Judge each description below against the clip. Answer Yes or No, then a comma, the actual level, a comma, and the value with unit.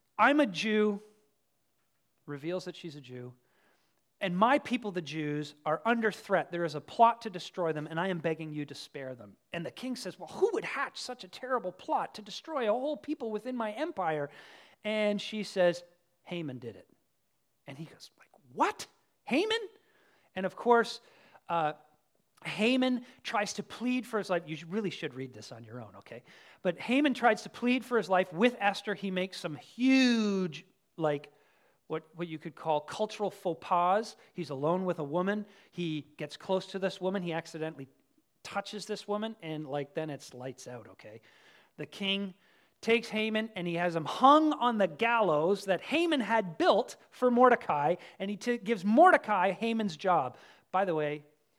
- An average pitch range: No, wide, 6.1 semitones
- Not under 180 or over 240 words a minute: Yes, average, 185 wpm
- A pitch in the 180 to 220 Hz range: Yes, high, 190 Hz